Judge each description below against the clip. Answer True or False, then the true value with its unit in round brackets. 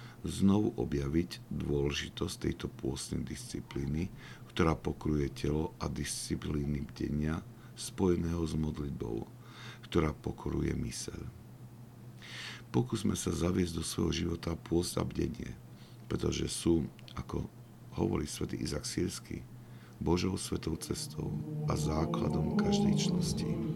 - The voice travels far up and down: True (7.2 semitones)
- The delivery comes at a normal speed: False (100 wpm)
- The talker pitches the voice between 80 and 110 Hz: True (85 Hz)